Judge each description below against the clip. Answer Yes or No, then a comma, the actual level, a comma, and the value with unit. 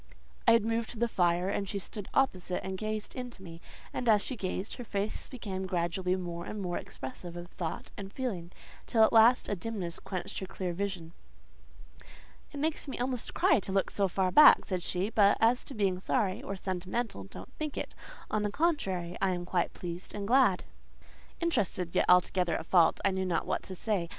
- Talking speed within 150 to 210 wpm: Yes, average, 200 wpm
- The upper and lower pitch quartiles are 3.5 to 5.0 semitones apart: Yes, average, 3.9 semitones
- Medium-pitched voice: No, high, 195 Hz